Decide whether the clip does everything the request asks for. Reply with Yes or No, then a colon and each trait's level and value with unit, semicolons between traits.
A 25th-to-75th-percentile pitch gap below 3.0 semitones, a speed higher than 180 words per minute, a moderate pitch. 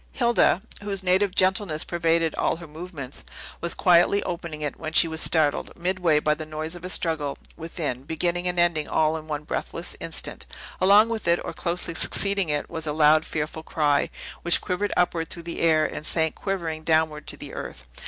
Yes: narrow, 2.5 semitones; average, 190 wpm; medium, 165 Hz